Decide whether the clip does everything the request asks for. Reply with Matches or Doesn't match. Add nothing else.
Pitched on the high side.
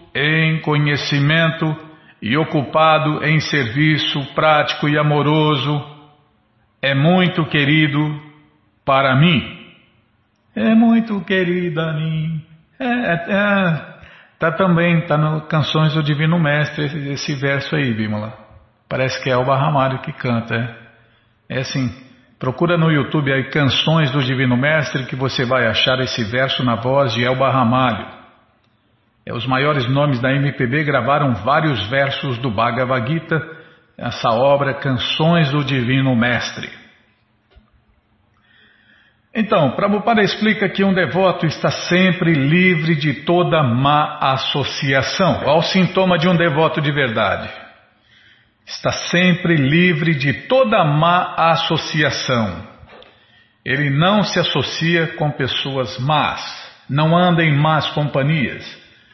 Doesn't match